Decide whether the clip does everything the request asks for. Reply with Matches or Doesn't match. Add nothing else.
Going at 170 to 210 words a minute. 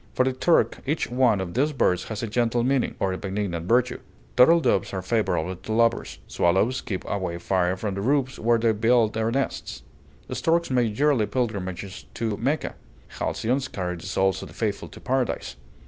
Matches